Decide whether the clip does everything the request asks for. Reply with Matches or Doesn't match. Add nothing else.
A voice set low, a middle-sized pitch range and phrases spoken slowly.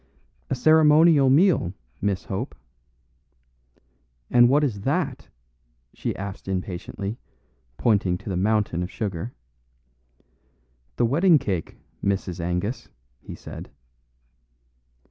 Doesn't match